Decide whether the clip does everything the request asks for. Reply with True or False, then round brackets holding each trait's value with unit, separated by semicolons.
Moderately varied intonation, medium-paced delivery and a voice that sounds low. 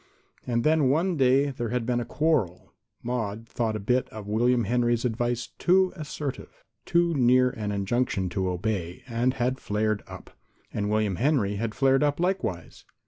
True (4.0 semitones; 170 wpm; 120 Hz)